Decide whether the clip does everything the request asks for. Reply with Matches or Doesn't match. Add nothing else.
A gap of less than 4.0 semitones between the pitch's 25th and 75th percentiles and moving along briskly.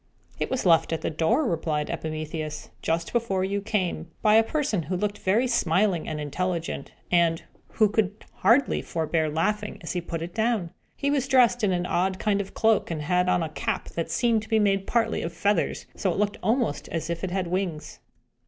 Doesn't match